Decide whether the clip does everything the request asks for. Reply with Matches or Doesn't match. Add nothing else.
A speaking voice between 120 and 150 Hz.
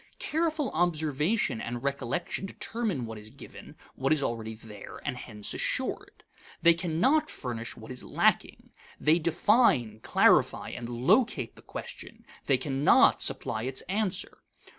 Matches